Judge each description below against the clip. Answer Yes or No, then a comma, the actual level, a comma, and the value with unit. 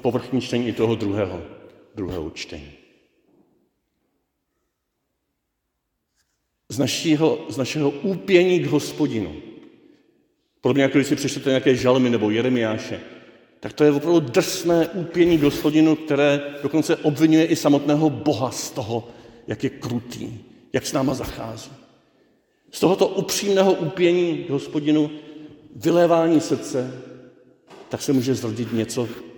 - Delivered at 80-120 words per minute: Yes, slow, 115 wpm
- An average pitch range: Yes, average, 4.5 semitones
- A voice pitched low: No, medium, 145 Hz